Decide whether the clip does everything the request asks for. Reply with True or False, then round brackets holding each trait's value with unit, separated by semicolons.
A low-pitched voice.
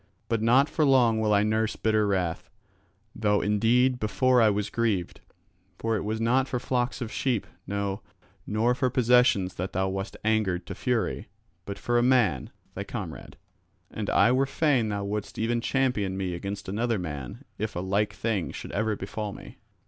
True (110 Hz)